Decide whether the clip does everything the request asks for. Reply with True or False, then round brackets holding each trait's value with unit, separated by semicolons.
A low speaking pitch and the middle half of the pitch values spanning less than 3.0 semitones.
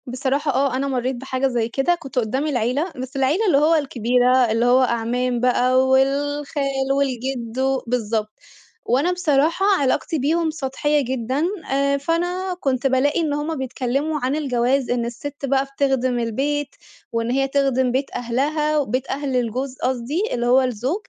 False (265 Hz; 2.6 semitones)